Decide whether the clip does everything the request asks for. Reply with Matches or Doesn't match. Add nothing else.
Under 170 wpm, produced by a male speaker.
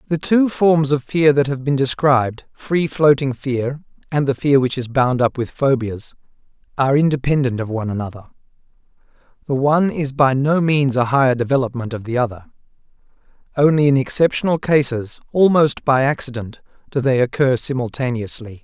Matches